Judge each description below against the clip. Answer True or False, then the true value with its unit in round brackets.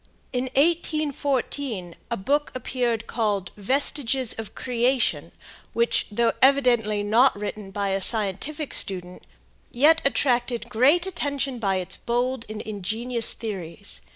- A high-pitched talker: True (235 Hz)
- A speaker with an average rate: False (120 wpm)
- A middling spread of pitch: True (4.6 semitones)